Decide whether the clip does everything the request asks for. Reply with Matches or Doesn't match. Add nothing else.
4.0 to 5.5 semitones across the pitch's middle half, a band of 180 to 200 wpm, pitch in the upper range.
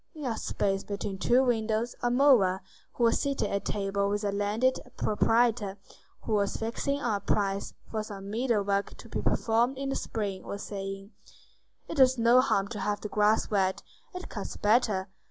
Doesn't match